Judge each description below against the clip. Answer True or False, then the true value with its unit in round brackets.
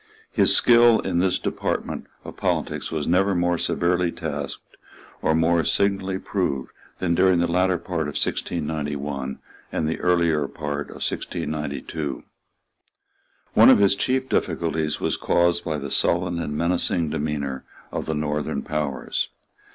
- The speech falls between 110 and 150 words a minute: True (140 wpm)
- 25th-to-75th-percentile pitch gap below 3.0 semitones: False (3.3 semitones)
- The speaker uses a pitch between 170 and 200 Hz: False (85 Hz)